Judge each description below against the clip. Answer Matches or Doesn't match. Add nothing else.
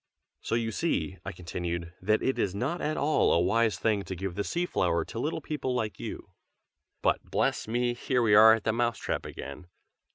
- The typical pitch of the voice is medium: Doesn't match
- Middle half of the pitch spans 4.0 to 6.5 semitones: Matches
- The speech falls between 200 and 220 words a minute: Matches